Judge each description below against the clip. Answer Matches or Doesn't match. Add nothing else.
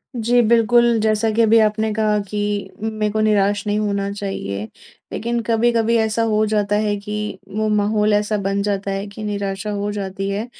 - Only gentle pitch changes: Matches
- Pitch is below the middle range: Doesn't match